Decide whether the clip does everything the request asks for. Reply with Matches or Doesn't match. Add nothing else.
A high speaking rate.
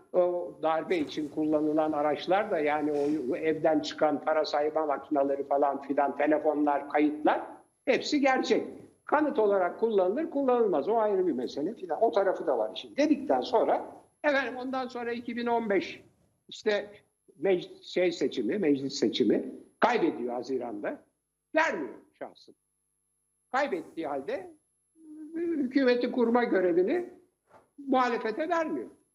Doesn't match